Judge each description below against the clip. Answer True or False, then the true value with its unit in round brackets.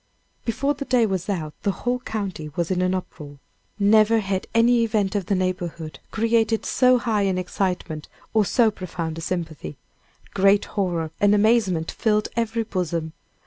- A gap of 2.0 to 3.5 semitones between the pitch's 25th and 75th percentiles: False (4.2 semitones)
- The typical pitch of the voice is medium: False (200 Hz)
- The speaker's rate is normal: True (160 wpm)